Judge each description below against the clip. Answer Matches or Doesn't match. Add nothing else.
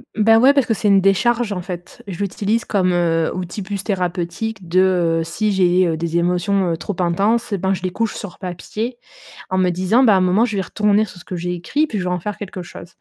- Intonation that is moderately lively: Matches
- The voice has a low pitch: Doesn't match